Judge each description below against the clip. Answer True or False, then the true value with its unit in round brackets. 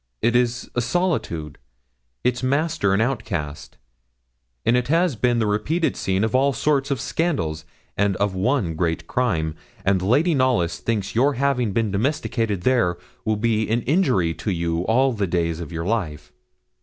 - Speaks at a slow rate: False (165 wpm)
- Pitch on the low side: True (110 Hz)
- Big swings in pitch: True (6.4 semitones)